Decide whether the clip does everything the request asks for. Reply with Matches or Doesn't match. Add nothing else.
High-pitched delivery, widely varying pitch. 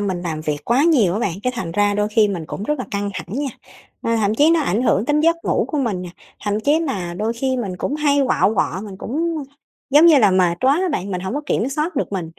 Matches